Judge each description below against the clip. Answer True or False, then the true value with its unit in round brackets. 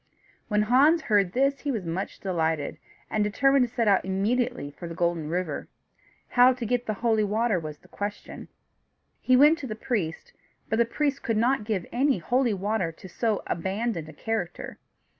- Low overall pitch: False (215 Hz)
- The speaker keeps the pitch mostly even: False (5.2 semitones)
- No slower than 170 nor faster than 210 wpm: True (180 wpm)